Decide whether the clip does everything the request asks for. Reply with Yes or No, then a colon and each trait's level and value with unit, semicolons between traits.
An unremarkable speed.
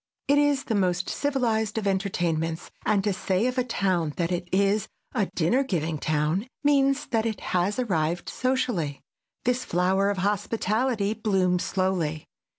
Yes: average, 155 wpm